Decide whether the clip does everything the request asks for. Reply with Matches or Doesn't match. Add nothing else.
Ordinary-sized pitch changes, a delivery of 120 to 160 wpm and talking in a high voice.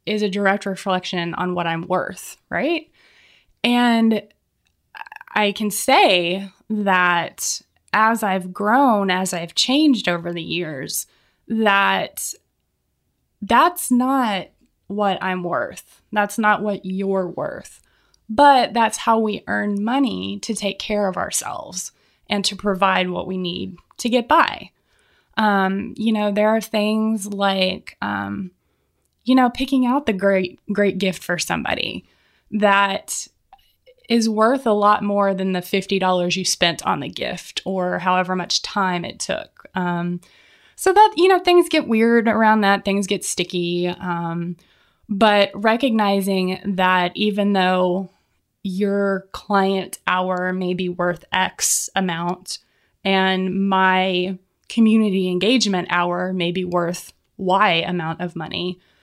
Matches